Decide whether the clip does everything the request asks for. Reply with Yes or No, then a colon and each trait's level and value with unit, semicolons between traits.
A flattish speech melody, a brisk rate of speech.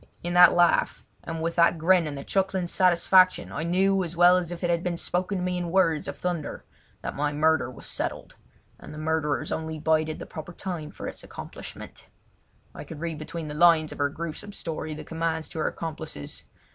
Yes: narrow, 2.1 semitones; fast, 210 wpm